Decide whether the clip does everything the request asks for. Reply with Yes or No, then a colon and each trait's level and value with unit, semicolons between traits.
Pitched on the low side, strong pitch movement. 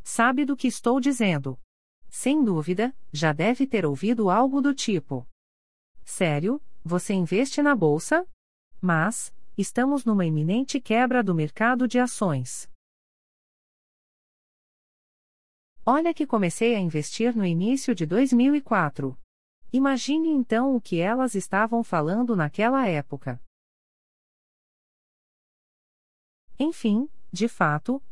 No: high, 220 Hz; wide, 8.4 semitones